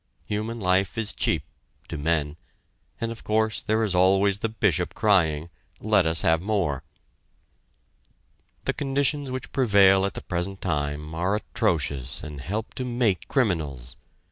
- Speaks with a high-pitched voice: No, very low, 95 Hz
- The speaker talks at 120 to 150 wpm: Yes, average, 140 wpm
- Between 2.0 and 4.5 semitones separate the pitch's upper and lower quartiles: No, average, 5.3 semitones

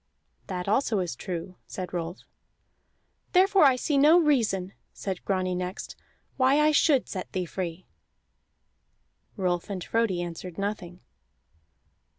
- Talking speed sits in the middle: No, slow, 125 wpm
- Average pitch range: No, wide, 6.4 semitones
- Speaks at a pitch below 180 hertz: No, high, 190 Hz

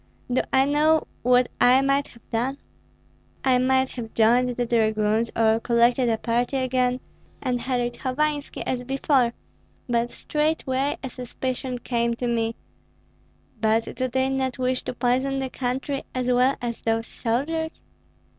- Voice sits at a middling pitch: No, very high, 250 Hz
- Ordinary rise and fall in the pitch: No, narrow, 2.1 semitones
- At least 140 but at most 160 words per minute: Yes, average, 145 wpm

